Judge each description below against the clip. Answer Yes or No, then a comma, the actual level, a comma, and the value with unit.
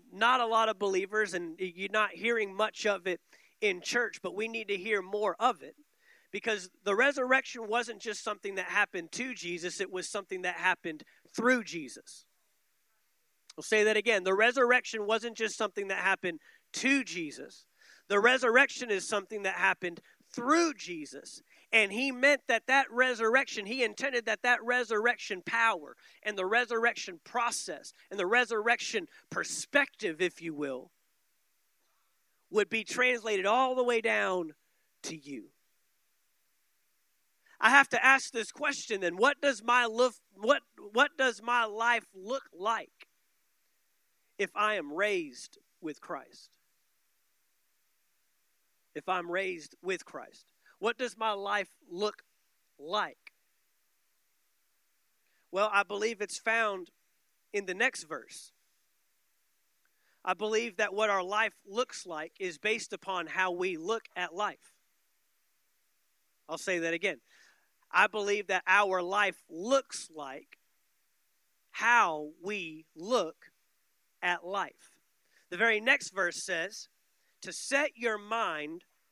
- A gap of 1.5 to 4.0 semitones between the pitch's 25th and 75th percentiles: No, average, 4.5 semitones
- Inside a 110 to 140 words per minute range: Yes, slow, 135 wpm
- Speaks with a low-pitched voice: No, high, 215 Hz